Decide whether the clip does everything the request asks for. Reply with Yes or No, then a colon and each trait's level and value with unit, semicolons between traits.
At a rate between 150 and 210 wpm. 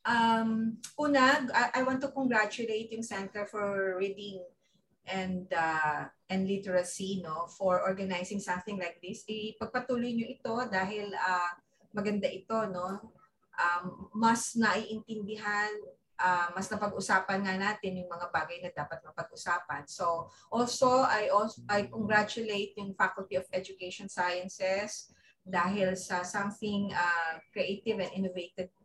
No: average, 125 wpm